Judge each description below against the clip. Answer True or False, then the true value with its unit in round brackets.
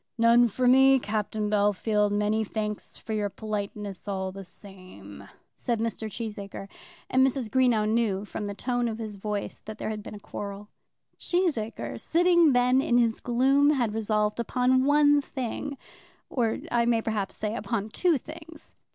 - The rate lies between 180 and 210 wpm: False (160 wpm)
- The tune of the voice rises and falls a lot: False (3.5 semitones)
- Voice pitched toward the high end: True (220 Hz)